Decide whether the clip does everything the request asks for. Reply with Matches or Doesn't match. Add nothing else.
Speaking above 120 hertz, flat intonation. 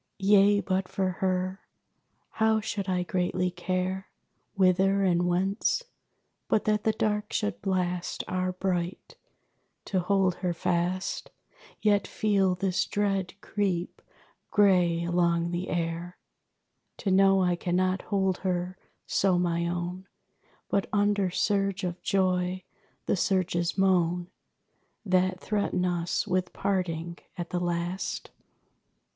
Matches